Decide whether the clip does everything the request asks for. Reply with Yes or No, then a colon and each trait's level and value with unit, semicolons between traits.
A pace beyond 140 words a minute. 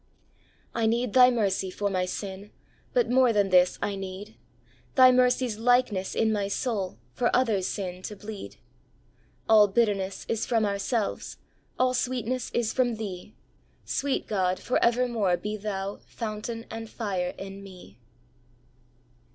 Yes: average, 150 wpm